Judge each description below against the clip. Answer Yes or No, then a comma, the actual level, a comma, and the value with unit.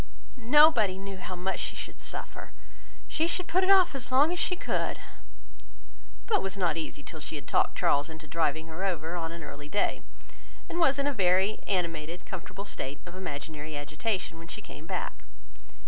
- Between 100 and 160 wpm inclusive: No, average, 185 wpm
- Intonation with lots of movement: Yes, wide, 7.4 semitones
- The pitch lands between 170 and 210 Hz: Yes, medium, 185 Hz